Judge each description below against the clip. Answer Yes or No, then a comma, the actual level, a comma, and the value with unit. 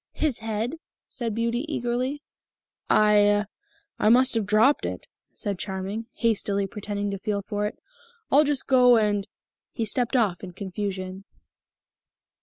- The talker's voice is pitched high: Yes, high, 215 Hz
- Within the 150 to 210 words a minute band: No, average, 140 wpm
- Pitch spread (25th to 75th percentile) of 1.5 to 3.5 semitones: Yes, average, 3.1 semitones